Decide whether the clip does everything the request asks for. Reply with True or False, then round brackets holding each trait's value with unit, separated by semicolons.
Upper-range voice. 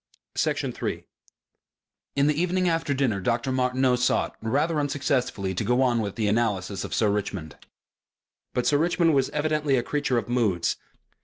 False (125 Hz)